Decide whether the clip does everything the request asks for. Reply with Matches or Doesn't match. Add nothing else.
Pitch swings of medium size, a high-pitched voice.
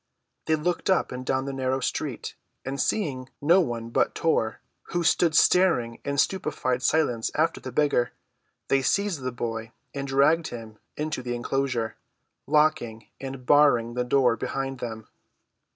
Doesn't match